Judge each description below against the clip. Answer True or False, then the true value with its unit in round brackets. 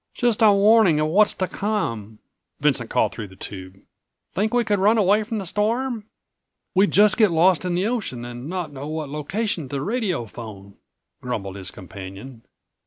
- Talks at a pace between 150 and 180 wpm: True (175 wpm)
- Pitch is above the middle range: False (175 Hz)